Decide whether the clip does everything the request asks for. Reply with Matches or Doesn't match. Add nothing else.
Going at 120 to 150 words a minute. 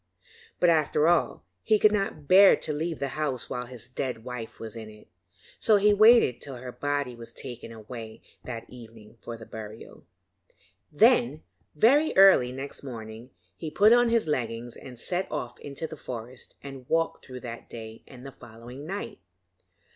Doesn't match